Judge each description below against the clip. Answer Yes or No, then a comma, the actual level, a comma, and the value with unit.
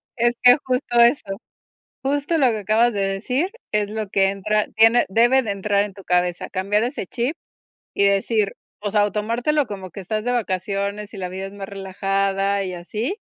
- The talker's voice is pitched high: Yes, high, 205 Hz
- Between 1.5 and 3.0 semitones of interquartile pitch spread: No, average, 3.4 semitones